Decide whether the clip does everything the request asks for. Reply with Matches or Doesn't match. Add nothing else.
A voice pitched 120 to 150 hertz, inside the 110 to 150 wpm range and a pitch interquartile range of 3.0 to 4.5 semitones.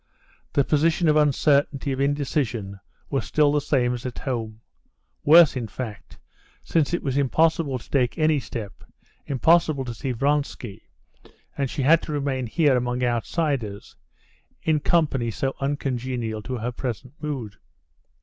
Matches